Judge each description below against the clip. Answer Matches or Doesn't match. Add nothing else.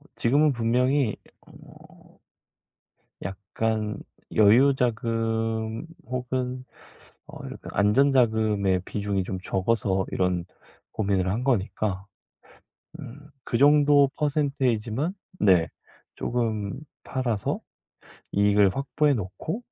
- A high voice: Doesn't match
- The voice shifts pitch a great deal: Doesn't match